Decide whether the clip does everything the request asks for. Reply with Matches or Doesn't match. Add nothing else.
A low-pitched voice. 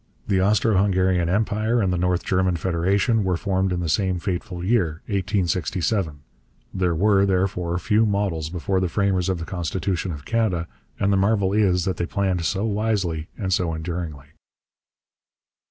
Matches